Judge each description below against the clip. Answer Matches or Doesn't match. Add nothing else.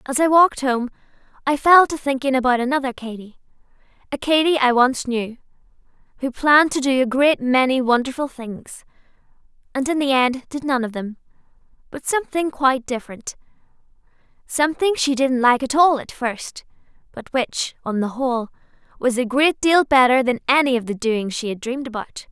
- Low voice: Doesn't match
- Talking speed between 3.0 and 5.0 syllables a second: Doesn't match